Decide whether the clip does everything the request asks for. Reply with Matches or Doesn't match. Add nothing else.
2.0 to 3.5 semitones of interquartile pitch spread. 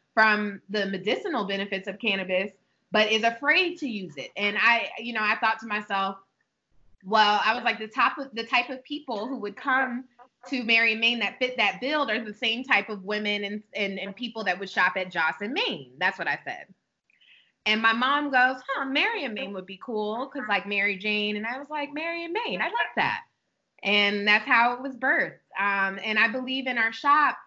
Doesn't match